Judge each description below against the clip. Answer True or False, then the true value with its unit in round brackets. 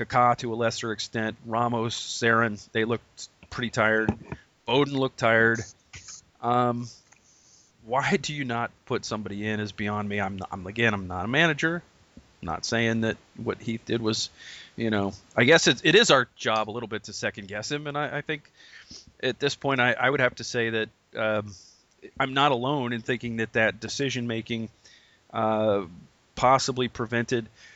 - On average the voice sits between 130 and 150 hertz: False (115 Hz)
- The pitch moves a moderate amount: False (2.2 semitones)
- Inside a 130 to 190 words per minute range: True (180 wpm)